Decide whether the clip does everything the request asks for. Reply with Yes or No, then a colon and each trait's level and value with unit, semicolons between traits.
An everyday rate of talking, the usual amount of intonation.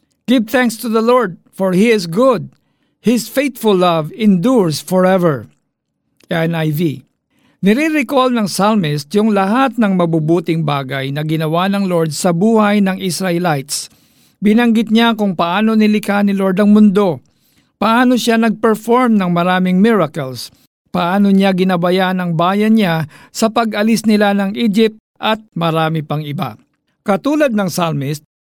Yes: average, 135 wpm; average, 4.7 semitones